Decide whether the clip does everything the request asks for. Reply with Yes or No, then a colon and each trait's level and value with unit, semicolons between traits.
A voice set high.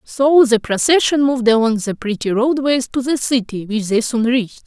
Yes: high, 245 Hz